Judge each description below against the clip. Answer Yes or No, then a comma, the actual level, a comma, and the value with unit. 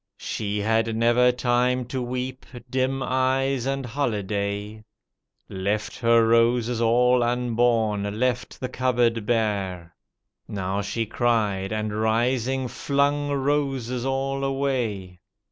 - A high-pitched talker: No, low, 120 Hz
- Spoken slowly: Yes, slow, 110 wpm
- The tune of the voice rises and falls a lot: No, average, 3.1 semitones